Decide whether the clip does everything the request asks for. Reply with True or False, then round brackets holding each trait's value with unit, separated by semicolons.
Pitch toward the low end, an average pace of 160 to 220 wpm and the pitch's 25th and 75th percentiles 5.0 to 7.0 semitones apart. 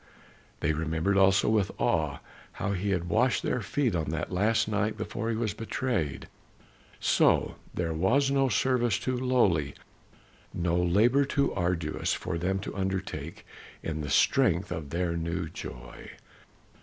False (95 Hz; 145 wpm; 5.4 semitones)